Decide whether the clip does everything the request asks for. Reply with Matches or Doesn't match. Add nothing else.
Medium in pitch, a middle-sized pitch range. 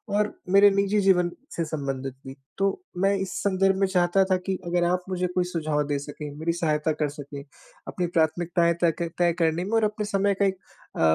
Matches